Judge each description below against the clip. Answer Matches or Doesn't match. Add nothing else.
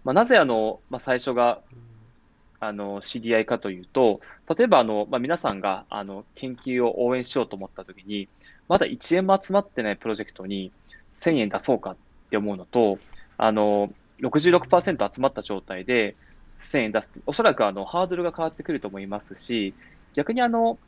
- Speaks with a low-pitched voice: Matches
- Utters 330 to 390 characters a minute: Matches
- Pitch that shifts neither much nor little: Matches